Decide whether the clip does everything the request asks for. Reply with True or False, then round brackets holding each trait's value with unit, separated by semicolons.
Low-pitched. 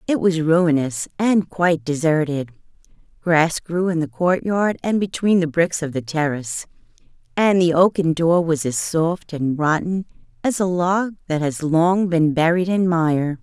False (165 Hz)